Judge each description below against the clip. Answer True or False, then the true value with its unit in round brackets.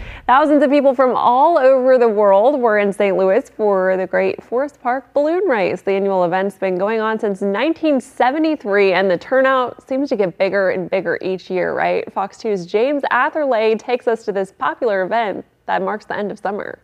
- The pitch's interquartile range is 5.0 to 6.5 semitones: True (5.3 semitones)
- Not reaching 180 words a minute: False (195 wpm)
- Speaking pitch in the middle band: False (220 Hz)